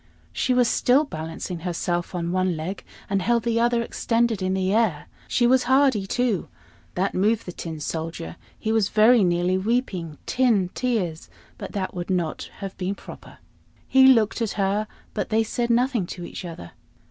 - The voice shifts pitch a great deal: No, average, 5.0 semitones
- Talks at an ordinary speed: Yes, average, 175 wpm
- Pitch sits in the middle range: No, high, 200 Hz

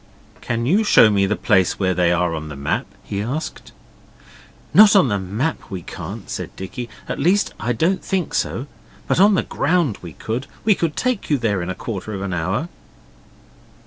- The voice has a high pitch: No, low, 115 Hz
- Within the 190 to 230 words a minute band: Yes, average, 195 wpm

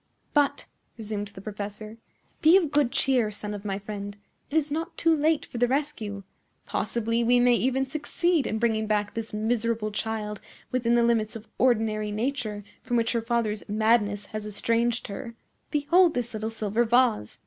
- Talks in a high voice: Yes, high, 230 Hz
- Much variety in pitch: No, average, 3.1 semitones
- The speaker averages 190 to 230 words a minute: No, average, 175 wpm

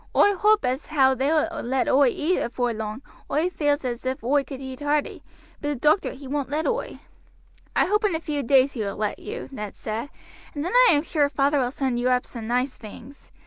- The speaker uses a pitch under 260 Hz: No, very high, 275 Hz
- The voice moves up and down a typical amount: Yes, average, 3.3 semitones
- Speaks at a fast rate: Yes, fast, 225 wpm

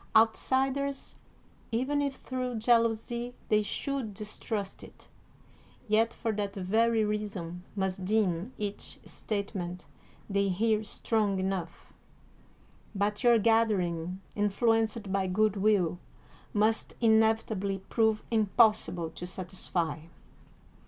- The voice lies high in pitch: Yes, high, 215 Hz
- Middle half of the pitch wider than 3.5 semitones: No, average, 2.9 semitones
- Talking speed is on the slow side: Yes, slow, 100 wpm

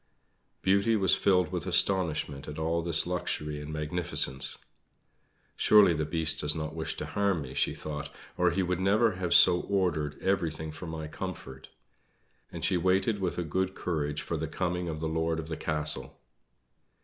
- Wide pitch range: No, average, 3.2 semitones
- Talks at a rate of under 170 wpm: No, average, 175 wpm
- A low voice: Yes, very low, 85 Hz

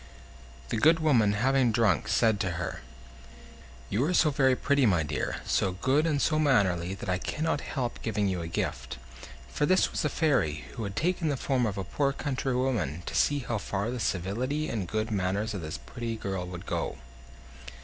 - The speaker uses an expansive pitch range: Yes, wide, 6.2 semitones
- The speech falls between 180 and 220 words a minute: Yes, average, 195 wpm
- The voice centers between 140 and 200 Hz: No, low, 115 Hz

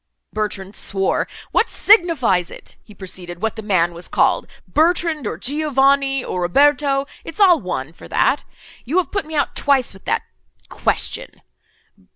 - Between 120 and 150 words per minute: Yes, average, 140 wpm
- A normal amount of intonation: No, wide, 8.1 semitones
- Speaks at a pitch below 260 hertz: No, very high, 265 Hz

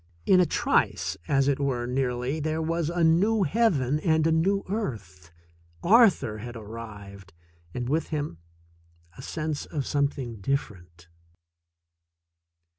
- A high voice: No, medium, 140 Hz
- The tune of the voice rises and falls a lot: Yes, wide, 6.0 semitones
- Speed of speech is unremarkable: No, slow, 125 wpm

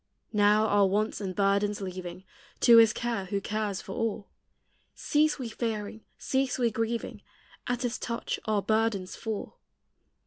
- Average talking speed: Yes, average, 145 wpm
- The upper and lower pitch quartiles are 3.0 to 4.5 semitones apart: No, narrow, 2.4 semitones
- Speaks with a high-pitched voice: Yes, high, 215 Hz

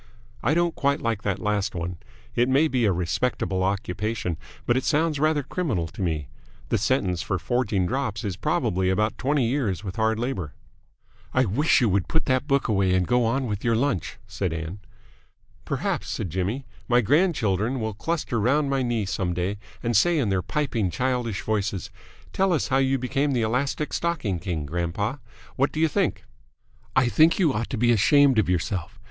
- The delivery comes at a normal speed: Yes, average, 190 wpm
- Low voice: Yes, low, 115 Hz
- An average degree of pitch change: No, wide, 6.1 semitones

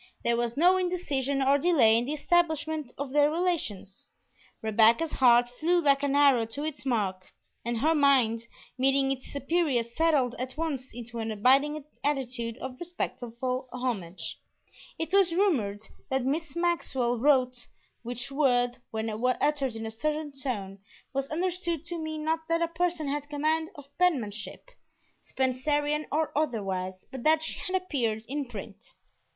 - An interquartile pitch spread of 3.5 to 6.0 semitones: Yes, average, 4.7 semitones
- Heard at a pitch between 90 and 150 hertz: No, very high, 275 Hz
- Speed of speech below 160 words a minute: Yes, average, 150 wpm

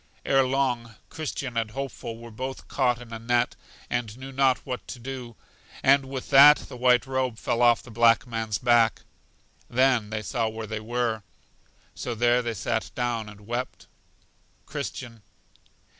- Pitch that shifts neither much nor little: No, narrow, 2.3 semitones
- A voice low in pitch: Yes, low, 120 Hz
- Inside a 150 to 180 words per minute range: Yes, average, 160 wpm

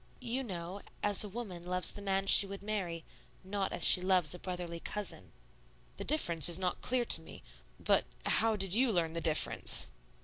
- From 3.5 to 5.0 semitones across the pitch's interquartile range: No, average, 3.1 semitones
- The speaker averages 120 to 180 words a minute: No, average, 190 wpm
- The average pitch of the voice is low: No, high, 190 Hz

